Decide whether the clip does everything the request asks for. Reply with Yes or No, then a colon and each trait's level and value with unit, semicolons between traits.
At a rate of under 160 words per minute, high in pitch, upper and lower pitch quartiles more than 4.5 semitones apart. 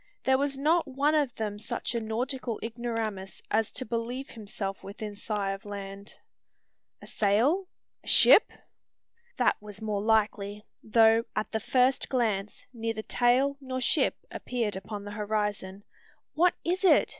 No: average, 145 wpm; high, 225 Hz; average, 3.8 semitones